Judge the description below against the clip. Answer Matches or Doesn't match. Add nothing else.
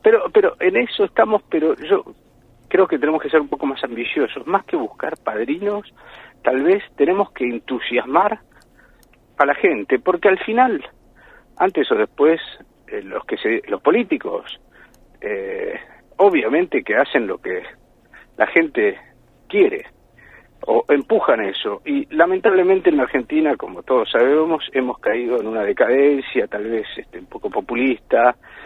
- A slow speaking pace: Doesn't match